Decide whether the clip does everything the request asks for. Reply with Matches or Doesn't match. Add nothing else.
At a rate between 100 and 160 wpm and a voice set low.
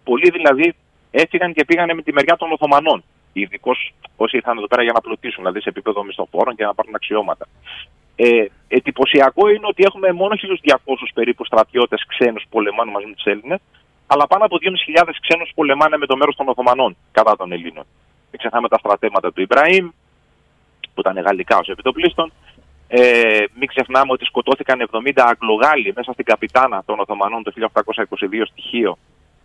Doesn't match